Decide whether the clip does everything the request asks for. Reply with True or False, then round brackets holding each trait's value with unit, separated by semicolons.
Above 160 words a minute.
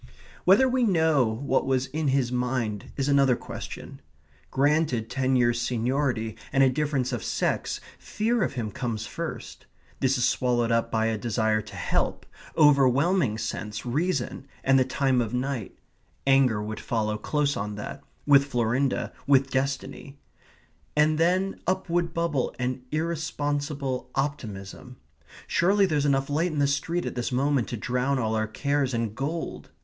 False (155 wpm)